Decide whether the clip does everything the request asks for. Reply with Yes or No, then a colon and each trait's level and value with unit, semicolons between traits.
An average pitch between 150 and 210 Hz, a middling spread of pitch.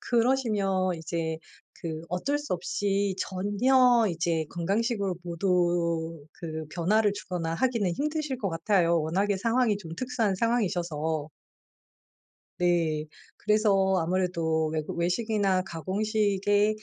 Yes: high, 190 Hz; average, 4.3 semitones